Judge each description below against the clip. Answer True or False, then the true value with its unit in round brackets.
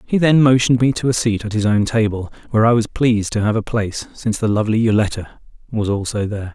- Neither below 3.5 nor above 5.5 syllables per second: False (6.6 syllables/s)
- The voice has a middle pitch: False (110 Hz)